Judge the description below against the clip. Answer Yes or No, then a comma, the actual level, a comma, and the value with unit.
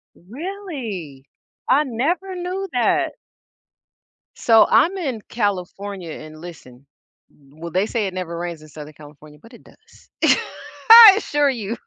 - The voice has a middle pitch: No, high, 210 Hz